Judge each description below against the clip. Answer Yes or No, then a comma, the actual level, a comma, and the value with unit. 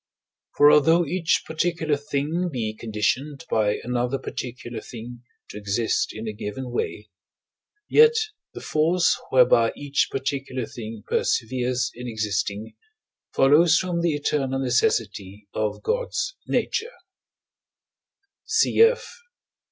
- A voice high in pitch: No, low, 130 Hz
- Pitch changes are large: Yes, wide, 5.9 semitones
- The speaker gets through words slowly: Yes, slow, 110 wpm